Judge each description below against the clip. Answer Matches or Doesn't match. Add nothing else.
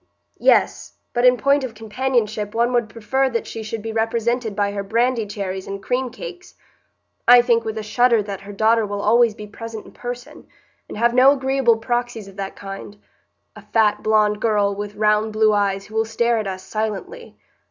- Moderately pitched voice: Doesn't match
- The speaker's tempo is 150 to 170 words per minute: Doesn't match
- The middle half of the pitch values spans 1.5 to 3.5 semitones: Matches